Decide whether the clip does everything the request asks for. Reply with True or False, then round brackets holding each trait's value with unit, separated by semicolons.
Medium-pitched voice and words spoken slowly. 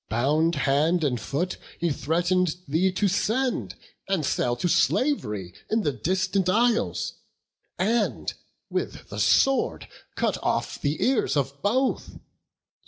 True (175 Hz; 125 wpm)